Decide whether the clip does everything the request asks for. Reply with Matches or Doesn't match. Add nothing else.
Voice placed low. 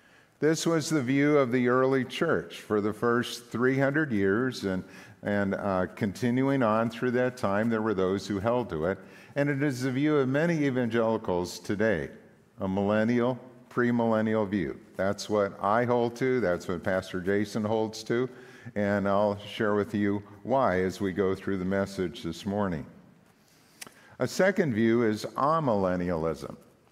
Matches